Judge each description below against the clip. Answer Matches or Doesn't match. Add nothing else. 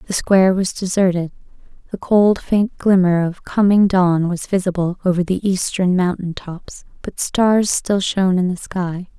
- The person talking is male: Doesn't match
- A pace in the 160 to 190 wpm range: Matches